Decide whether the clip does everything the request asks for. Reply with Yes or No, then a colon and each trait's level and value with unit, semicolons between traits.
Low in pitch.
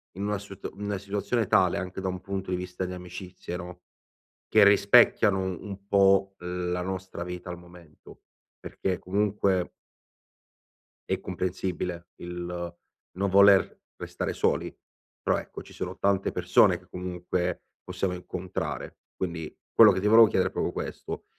Yes: very low, 95 Hz